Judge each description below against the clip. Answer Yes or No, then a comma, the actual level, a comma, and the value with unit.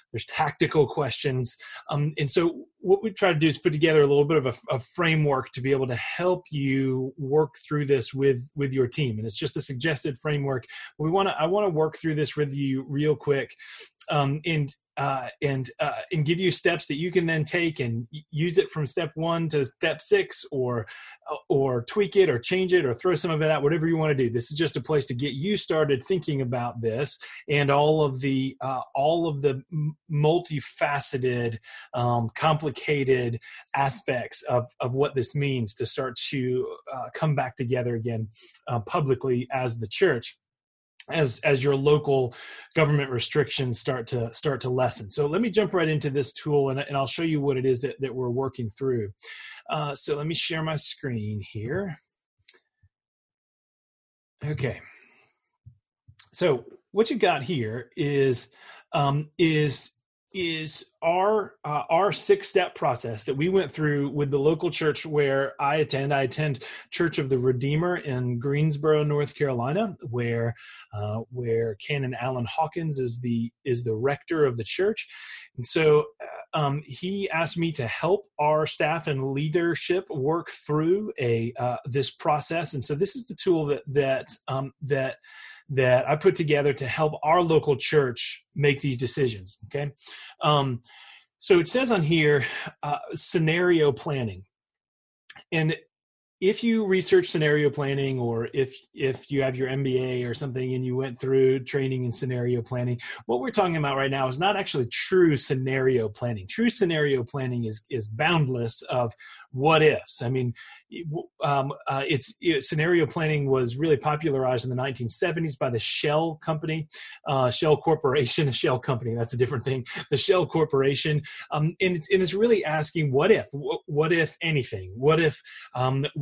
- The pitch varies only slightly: No, average, 3.8 semitones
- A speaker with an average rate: Yes, average, 175 wpm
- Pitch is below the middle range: No, medium, 145 Hz